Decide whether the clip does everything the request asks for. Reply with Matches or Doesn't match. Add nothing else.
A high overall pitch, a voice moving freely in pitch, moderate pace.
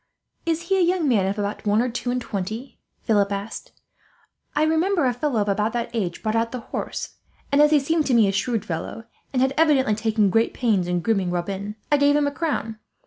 Doesn't match